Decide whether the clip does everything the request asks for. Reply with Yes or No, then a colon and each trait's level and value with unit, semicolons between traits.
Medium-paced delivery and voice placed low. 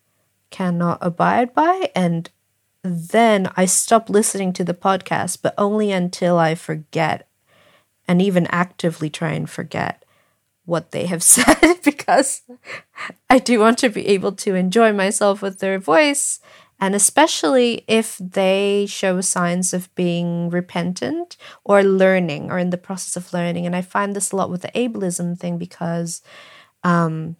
No: average, 150 wpm; medium, 185 Hz